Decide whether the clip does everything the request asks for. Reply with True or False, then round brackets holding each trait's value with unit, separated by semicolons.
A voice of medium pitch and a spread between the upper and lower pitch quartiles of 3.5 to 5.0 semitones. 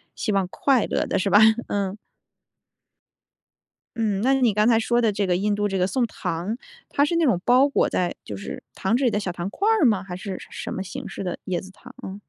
False (205 Hz; 4.1 semitones)